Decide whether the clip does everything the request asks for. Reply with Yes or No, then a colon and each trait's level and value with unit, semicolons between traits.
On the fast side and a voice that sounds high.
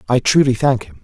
No: fast, 235 wpm; low, 120 Hz